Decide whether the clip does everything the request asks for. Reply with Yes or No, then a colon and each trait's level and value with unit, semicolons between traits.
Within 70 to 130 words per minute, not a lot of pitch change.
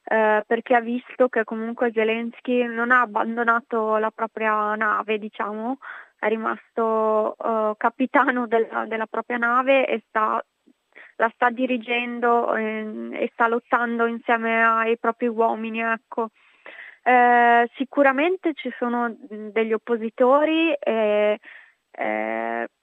Yes: slow, 115 wpm; narrow, 1.8 semitones